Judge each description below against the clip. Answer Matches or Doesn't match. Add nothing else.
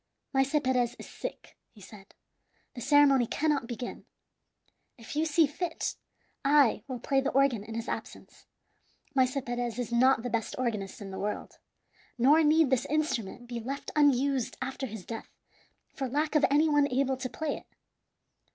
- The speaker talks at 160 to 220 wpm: Matches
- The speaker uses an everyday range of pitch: Matches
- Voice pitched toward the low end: Doesn't match